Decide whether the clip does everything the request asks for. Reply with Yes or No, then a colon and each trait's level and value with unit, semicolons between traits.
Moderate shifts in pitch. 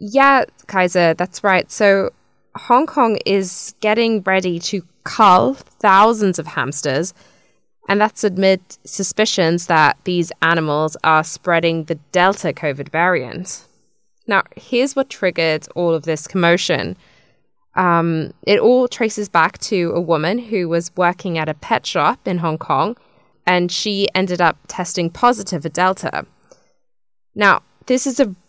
Yes: average, 3.9 semitones